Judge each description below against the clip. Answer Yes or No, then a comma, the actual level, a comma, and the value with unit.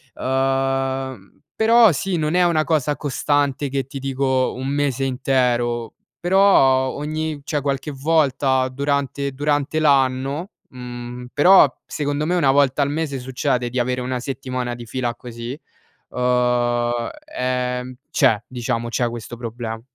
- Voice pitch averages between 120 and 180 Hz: Yes, low, 135 Hz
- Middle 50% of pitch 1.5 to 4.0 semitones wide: Yes, narrow, 2.6 semitones